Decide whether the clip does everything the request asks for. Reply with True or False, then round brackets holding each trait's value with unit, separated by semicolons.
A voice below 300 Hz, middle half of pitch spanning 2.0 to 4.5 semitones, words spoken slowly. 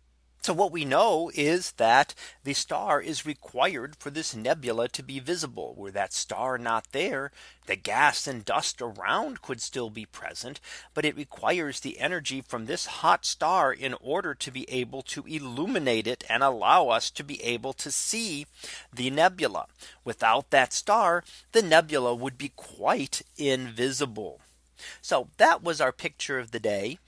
False (135 Hz; 4.1 semitones; 165 wpm)